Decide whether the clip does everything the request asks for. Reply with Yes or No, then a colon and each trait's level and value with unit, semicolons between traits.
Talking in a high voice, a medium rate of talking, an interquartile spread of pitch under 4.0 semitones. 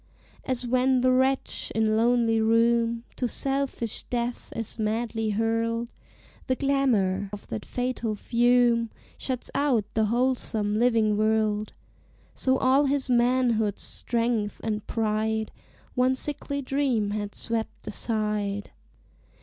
No: high, 230 Hz; slow, 115 wpm; average, 2.7 semitones